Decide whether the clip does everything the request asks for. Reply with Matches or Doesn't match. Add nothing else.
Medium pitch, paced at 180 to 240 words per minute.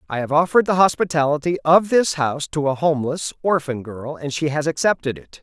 Matches